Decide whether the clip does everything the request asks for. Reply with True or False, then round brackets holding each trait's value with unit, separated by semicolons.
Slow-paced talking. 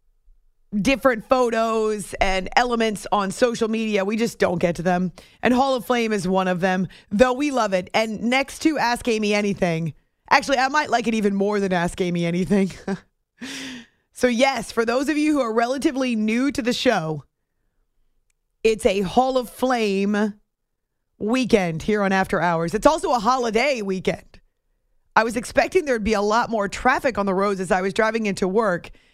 False (185 wpm)